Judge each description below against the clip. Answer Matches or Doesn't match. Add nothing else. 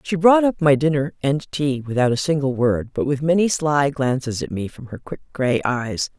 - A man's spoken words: Doesn't match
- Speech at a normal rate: Doesn't match